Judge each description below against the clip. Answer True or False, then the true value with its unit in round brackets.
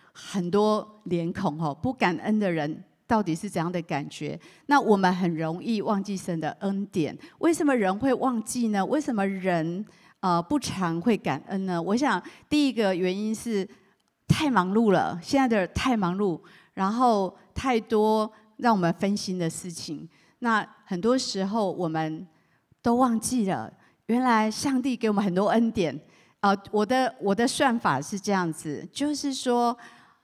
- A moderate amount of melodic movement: True (4.8 semitones)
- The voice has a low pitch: False (200 Hz)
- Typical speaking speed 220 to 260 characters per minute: True (230 characters per minute)